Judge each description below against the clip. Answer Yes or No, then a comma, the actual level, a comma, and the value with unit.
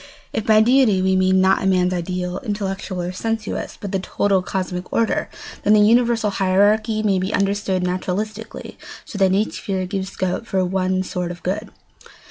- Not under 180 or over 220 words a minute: No, average, 160 wpm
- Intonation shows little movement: Yes, narrow, 2.3 semitones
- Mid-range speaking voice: No, high, 195 Hz